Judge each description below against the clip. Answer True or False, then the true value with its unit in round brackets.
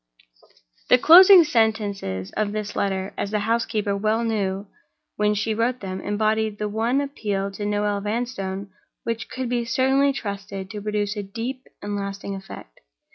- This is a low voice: False (210 Hz)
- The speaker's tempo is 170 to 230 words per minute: False (145 wpm)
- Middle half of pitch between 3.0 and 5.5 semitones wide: False (2.5 semitones)